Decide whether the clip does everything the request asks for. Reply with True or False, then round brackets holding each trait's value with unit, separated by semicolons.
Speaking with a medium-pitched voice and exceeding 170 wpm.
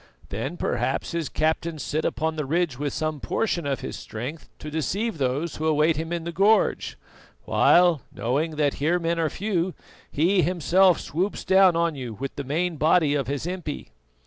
True (160 Hz; 180 wpm)